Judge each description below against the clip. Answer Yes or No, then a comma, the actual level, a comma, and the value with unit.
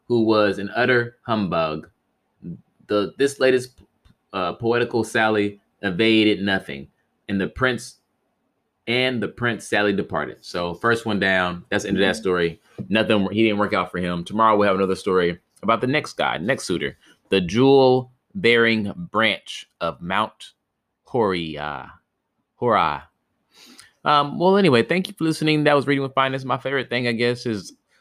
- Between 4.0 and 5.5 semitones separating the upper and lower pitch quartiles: Yes, average, 4.7 semitones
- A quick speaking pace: No, average, 160 wpm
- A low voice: Yes, low, 110 Hz